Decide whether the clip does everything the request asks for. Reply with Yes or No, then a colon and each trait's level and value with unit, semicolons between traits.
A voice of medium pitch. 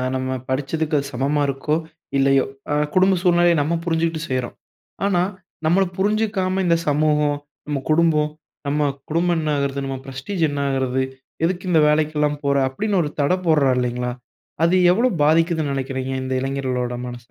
Yes: medium, 150 Hz